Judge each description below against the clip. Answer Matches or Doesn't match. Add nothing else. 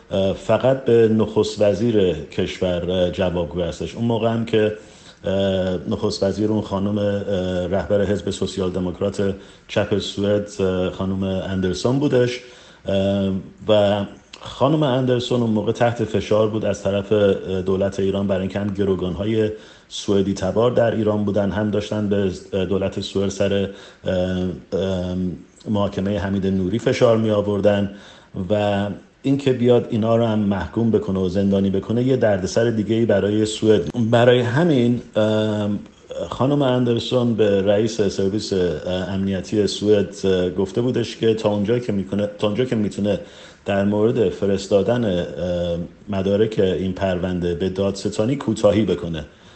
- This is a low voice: Matches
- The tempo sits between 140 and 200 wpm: Doesn't match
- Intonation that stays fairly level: Matches